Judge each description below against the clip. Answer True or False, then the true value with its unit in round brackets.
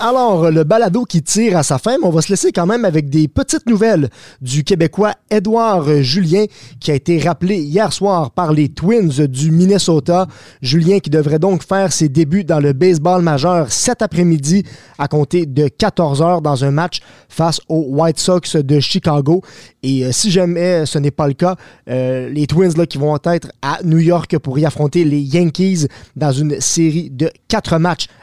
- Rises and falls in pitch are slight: False (3.7 semitones)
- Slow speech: False (195 wpm)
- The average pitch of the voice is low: False (165 Hz)